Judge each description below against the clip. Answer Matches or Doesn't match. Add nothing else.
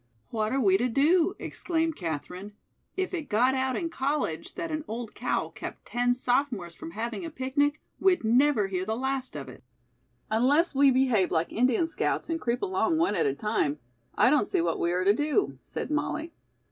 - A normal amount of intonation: Doesn't match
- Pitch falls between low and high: Doesn't match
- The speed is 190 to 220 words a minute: Matches